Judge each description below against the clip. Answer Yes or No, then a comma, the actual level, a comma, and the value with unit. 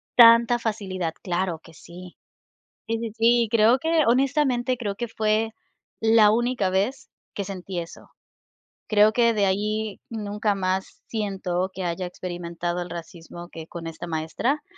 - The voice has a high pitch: Yes, high, 205 Hz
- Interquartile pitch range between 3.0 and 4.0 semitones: No, average, 4.5 semitones